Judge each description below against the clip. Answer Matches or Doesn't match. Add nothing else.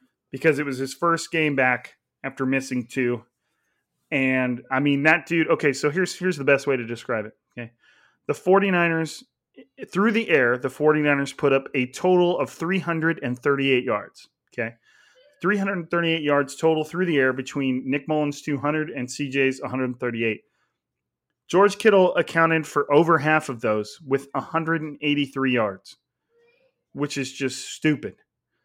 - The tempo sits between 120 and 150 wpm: Matches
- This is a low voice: Doesn't match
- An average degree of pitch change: Matches